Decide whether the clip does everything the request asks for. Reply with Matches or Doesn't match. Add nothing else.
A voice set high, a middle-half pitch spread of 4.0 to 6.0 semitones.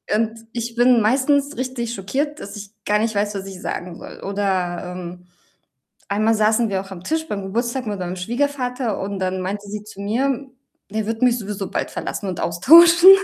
Matches